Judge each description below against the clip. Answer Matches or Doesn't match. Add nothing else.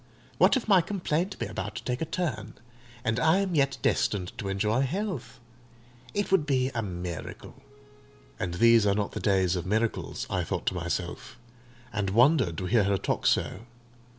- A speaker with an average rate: Matches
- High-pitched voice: Doesn't match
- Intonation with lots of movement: Matches